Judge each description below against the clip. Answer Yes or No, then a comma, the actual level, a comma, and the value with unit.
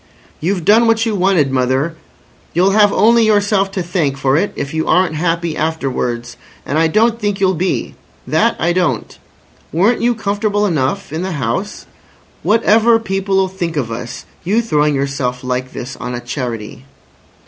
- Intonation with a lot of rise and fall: Yes, wide, 6.9 semitones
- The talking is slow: No, average, 160 wpm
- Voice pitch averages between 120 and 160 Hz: No, medium, 175 Hz